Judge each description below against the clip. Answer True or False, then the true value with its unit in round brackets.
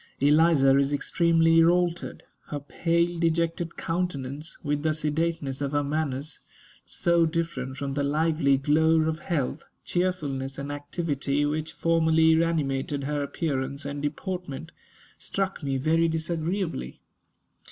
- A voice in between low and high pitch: True (155 Hz)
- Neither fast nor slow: False (120 wpm)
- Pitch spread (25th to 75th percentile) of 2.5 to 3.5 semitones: True (2.9 semitones)